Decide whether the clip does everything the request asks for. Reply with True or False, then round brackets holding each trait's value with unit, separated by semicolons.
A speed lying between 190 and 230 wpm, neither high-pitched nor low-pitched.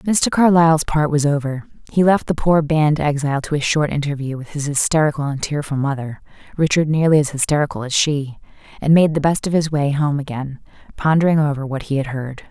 True (200 wpm; 150 Hz)